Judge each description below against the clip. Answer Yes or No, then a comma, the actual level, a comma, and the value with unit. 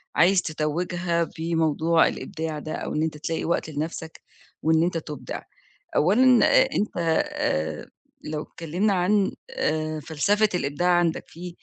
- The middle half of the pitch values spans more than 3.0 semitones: No, narrow, 2.4 semitones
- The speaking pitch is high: No, medium, 165 Hz